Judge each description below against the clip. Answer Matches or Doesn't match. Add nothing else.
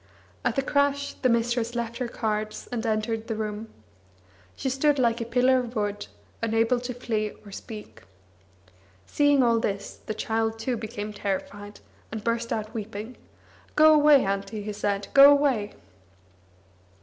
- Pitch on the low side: Doesn't match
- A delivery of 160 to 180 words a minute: Doesn't match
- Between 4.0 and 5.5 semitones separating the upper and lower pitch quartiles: Doesn't match